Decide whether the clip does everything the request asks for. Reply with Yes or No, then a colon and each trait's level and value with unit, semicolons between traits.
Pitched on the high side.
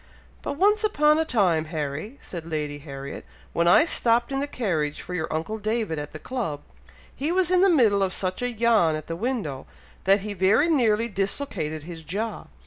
Yes: high, 200 Hz